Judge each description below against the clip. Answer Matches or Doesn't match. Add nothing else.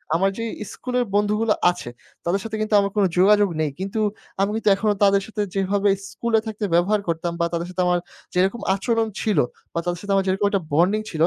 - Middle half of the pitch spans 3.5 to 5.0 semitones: Doesn't match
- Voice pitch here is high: Matches